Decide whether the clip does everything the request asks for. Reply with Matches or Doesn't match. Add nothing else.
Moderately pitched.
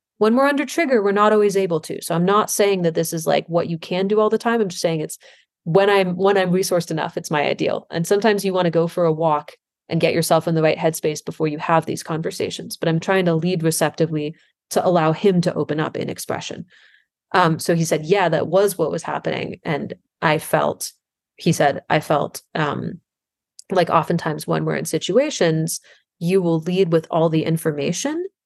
Matches